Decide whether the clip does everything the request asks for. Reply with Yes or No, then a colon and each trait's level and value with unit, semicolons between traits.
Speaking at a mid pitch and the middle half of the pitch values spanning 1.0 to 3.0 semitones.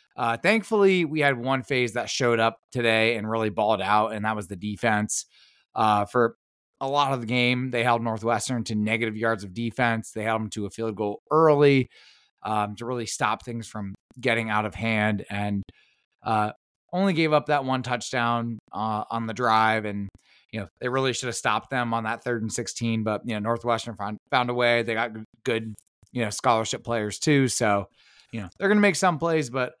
No: low, 115 Hz; average, 2.7 semitones